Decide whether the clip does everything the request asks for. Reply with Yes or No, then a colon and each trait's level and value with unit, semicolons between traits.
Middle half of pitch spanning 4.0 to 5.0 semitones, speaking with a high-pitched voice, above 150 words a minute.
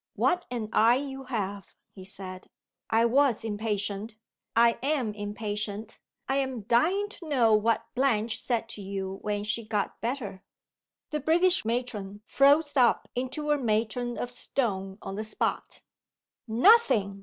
No: average, 4.4 semitones; high, 230 Hz; average, 145 wpm